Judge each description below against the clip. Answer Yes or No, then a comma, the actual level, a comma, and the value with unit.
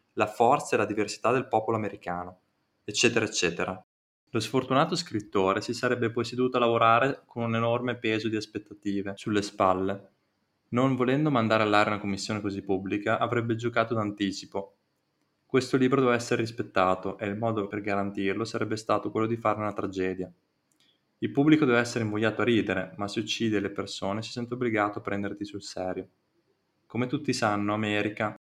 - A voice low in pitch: Yes, low, 105 Hz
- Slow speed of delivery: No, average, 165 wpm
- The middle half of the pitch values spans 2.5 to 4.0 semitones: Yes, average, 2.9 semitones